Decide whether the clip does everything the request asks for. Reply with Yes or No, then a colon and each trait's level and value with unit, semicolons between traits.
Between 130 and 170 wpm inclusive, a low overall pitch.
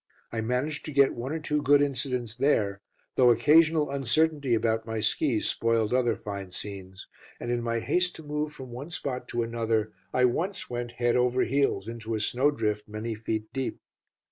No: average, 180 wpm; low, 120 Hz